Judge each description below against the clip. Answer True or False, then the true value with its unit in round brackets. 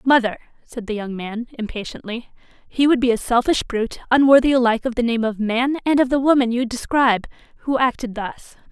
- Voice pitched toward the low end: False (240 Hz)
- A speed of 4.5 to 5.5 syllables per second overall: False (5.9 syllables/s)